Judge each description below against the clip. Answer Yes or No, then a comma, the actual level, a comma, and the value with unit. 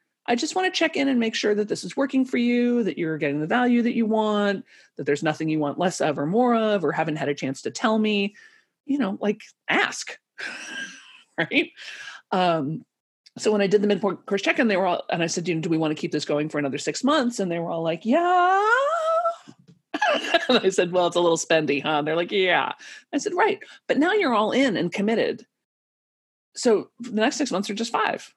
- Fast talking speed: Yes, fast, 230 wpm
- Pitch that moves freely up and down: Yes, wide, 8.3 semitones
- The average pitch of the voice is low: No, high, 215 Hz